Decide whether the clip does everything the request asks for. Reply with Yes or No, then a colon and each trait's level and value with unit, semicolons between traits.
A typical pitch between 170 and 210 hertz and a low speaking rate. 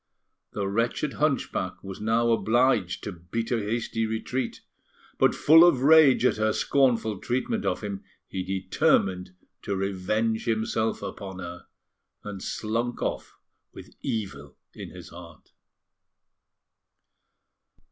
No: low, 110 Hz; slow, 120 wpm